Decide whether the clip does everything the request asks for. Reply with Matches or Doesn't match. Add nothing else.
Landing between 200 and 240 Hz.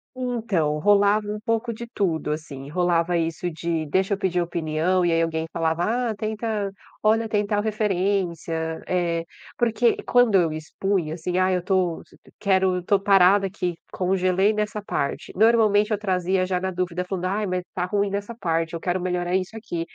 Doesn't match